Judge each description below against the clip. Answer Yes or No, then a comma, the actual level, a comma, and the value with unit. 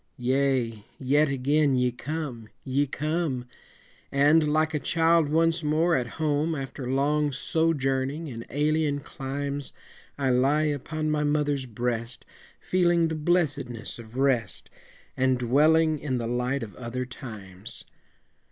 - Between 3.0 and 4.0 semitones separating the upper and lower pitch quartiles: Yes, average, 3.4 semitones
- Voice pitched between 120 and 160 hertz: Yes, medium, 140 Hz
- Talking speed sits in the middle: No, slow, 130 wpm